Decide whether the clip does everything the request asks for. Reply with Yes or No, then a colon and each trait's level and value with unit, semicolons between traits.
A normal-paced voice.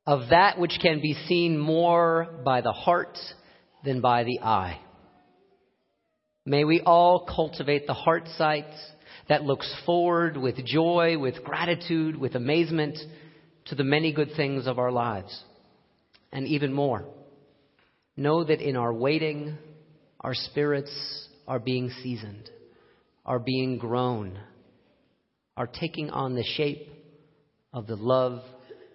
No: slow, 130 wpm